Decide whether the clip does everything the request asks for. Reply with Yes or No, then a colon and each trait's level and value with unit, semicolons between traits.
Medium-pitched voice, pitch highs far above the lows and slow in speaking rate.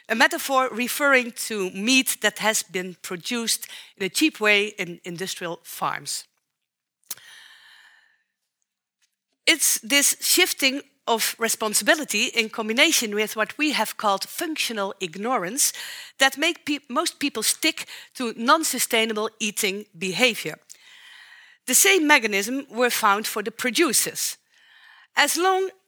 No: high, 245 Hz; wide, 6.8 semitones; slow, 120 wpm